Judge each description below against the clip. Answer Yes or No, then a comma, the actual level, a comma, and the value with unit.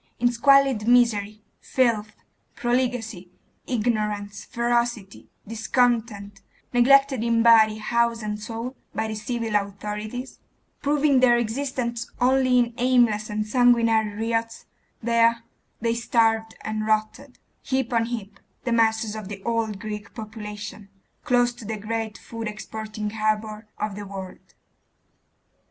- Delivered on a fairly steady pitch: Yes, narrow, 2.2 semitones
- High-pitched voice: Yes, high, 225 Hz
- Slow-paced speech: Yes, slow, 120 wpm